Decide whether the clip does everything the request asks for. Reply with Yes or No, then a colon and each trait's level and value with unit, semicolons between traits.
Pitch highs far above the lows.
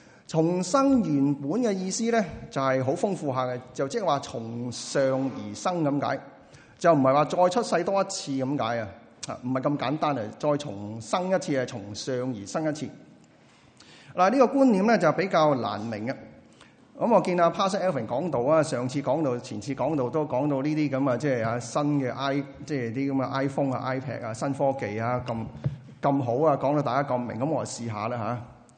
No: average, 4.3 semitones